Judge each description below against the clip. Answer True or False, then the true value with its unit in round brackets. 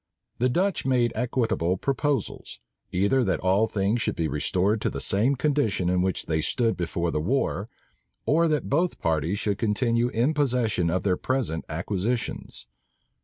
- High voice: False (110 Hz)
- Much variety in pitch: True (6.0 semitones)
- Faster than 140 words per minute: True (160 wpm)